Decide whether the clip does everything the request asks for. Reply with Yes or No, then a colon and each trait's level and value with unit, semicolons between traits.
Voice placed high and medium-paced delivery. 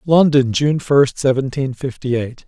No: low, 135 Hz; average, 145 wpm